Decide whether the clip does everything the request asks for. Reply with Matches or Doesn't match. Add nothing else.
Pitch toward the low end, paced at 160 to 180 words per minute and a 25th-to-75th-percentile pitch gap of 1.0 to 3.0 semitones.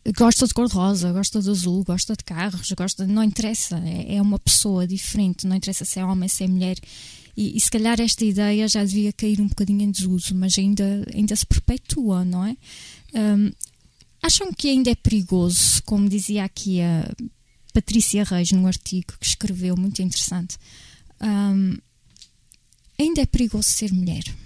Doesn't match